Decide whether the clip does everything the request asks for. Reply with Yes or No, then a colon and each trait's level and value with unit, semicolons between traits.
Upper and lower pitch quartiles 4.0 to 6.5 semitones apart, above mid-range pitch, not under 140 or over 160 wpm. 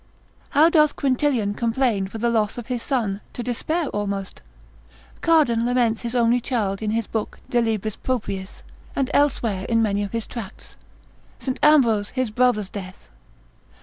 No: average, 3.5 semitones; high, 230 Hz; average, 155 wpm